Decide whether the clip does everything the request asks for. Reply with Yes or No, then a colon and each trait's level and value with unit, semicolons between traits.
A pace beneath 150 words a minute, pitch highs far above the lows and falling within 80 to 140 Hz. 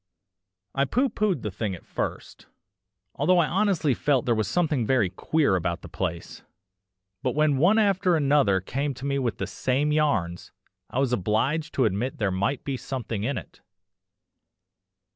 No: average, 165 wpm; wide, 6.2 semitones; low, 135 Hz